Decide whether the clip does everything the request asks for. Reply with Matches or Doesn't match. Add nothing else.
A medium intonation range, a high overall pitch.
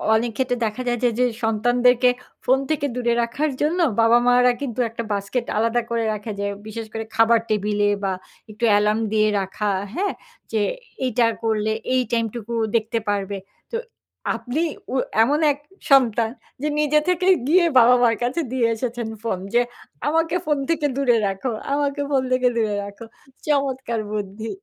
Matches